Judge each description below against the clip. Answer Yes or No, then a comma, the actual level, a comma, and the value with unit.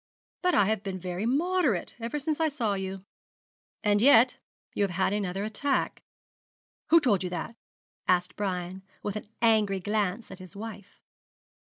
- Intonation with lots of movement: No, average, 3.7 semitones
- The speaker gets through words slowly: No, average, 160 wpm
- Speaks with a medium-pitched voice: No, high, 205 Hz